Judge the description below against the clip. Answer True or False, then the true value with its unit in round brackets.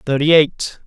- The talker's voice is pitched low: False (150 Hz)